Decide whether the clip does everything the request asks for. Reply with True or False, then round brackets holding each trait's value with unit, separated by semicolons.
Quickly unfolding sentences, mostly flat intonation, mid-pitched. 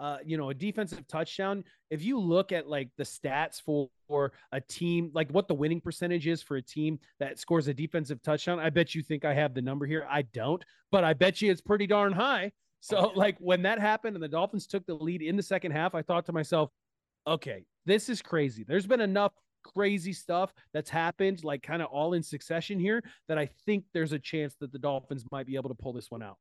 False (235 wpm; 4.6 semitones; 165 Hz)